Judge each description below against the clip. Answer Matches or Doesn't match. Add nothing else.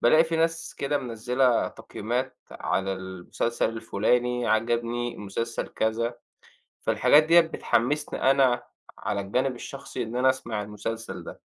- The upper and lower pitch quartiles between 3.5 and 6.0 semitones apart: Doesn't match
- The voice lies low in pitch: Matches